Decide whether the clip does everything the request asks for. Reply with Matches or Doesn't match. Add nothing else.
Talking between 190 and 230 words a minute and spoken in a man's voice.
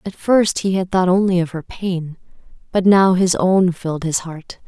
Doesn't match